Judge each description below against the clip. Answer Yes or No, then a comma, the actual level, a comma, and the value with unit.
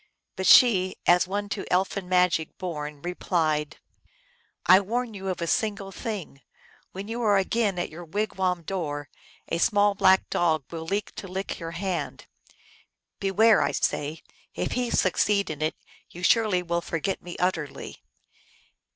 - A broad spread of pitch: No, average, 3.2 semitones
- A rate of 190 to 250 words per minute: No, average, 160 wpm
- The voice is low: No, medium, 185 Hz